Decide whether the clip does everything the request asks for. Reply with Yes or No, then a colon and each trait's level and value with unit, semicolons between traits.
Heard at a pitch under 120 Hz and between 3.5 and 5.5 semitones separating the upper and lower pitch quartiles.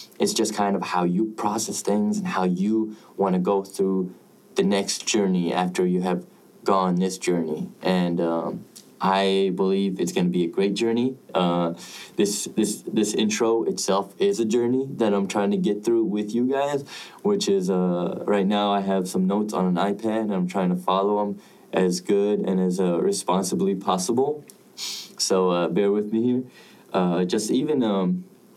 Yes: low, 100 Hz; average, 4.0 semitones